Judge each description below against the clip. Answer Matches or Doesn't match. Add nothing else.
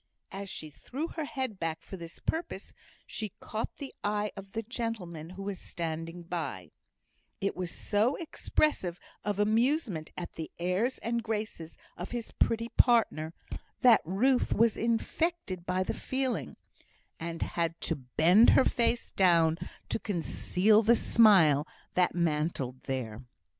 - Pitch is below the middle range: Doesn't match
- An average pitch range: Doesn't match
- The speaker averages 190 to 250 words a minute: Doesn't match